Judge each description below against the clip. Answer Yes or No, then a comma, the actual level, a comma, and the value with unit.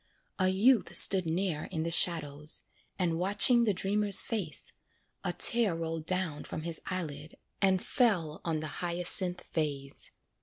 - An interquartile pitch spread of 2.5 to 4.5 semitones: Yes, average, 3.4 semitones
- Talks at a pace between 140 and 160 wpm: Yes, average, 145 wpm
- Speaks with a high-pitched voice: No, medium, 175 Hz